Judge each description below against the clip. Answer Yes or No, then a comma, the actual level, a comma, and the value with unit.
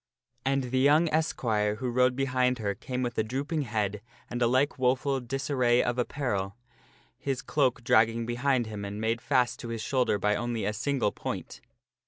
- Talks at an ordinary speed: Yes, average, 185 wpm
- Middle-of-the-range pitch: No, low, 125 Hz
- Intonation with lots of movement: No, average, 3.1 semitones